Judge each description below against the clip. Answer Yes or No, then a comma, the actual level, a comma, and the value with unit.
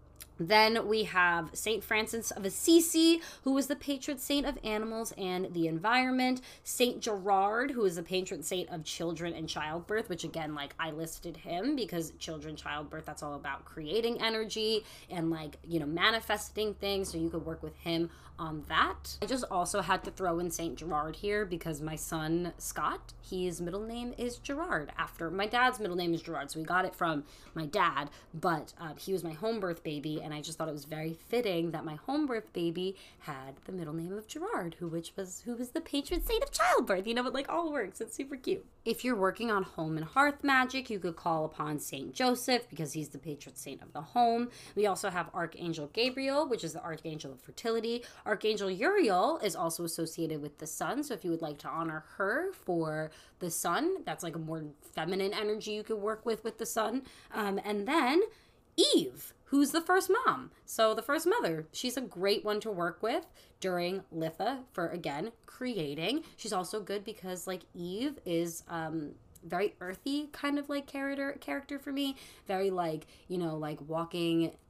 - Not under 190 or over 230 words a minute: Yes, average, 200 wpm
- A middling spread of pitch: No, wide, 6.6 semitones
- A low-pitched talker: No, high, 190 Hz